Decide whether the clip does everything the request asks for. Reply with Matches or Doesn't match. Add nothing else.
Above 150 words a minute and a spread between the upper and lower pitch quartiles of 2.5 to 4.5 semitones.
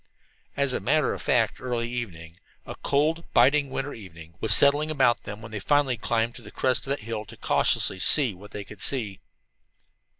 Doesn't match